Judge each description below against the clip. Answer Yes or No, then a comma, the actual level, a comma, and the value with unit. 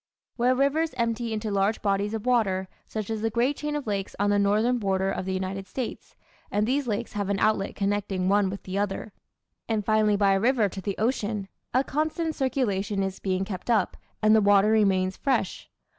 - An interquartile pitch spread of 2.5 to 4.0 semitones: Yes, average, 3.2 semitones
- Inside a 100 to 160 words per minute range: No, fast, 205 wpm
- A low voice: No, high, 210 Hz